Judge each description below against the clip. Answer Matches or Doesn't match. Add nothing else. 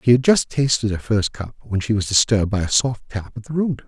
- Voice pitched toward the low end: Matches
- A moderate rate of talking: Doesn't match